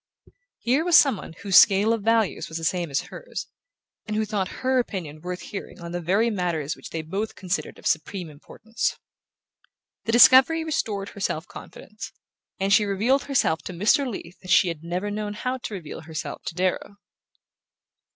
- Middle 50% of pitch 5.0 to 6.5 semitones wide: No, average, 4.6 semitones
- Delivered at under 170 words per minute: No, average, 180 wpm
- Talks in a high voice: Yes, high, 200 Hz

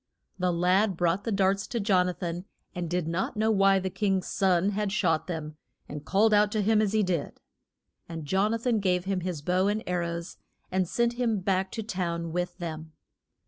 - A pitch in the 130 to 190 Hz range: Yes, medium, 185 Hz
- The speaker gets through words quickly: Yes, fast, 210 wpm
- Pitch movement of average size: Yes, average, 3.0 semitones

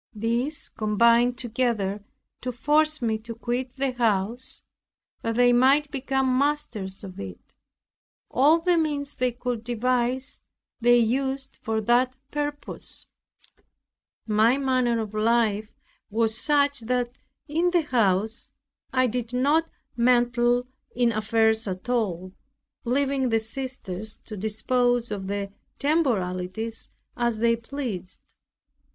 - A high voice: Yes, high, 240 Hz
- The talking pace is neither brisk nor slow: No, slow, 120 wpm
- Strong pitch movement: No, average, 3.1 semitones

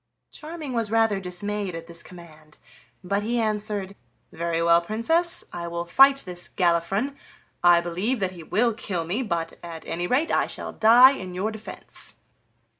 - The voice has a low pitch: No, high, 195 Hz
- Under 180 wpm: Yes, average, 165 wpm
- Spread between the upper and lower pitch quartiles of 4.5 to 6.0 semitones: Yes, average, 4.9 semitones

